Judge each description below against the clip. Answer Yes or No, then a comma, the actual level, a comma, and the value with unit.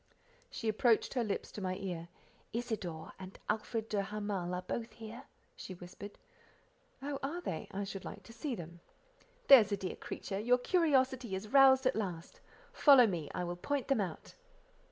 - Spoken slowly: No, average, 170 wpm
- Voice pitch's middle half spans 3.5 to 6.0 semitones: Yes, average, 5.1 semitones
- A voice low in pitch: No, high, 210 Hz